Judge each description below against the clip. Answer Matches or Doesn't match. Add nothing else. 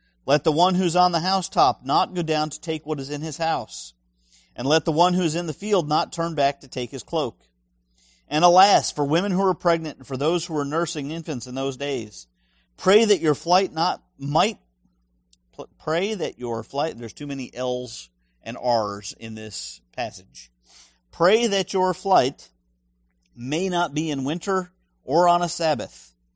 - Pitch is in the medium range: Matches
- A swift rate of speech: Doesn't match